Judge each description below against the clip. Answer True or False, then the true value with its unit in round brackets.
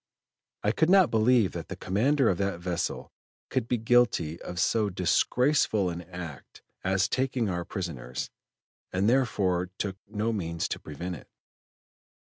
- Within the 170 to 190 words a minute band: False (145 wpm)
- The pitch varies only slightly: False (5.0 semitones)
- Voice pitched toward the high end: False (95 Hz)